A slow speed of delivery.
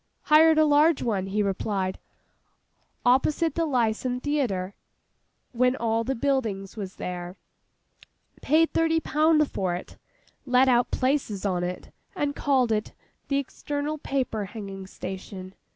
Yes: slow, 125 wpm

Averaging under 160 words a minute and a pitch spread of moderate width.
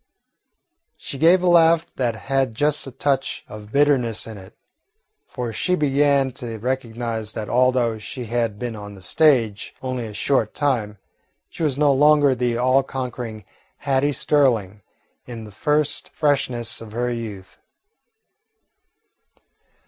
Yes: average, 140 wpm; average, 4.0 semitones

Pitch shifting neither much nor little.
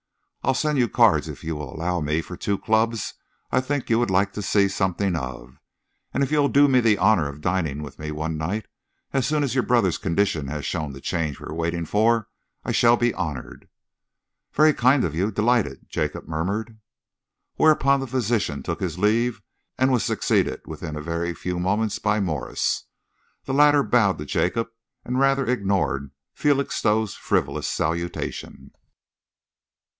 No: wide, 6.9 semitones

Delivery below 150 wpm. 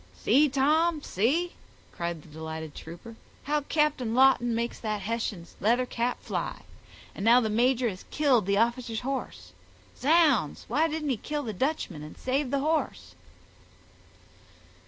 Yes: average, 140 wpm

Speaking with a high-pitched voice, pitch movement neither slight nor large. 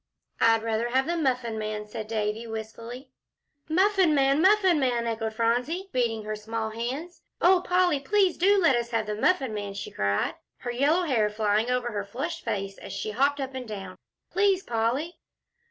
No: high, 240 Hz; wide, 6.3 semitones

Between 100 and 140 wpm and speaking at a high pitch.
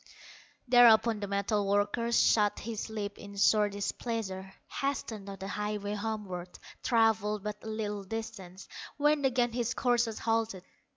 Yes: slow, 135 wpm; high, 210 Hz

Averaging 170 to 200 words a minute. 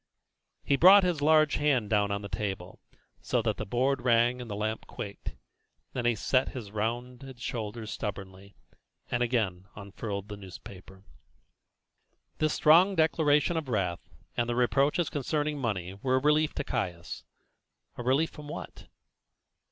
No: average, 155 wpm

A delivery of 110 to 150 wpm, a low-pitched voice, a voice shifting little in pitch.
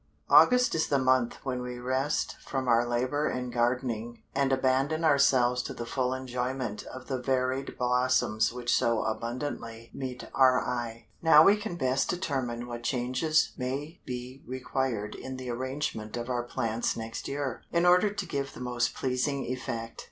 No: average, 165 wpm; low, 130 Hz; narrow, 2.2 semitones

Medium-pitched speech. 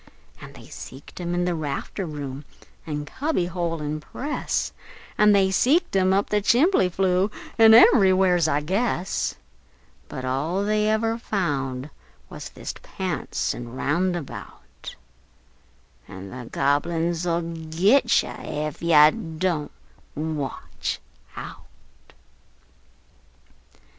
Yes: medium, 175 Hz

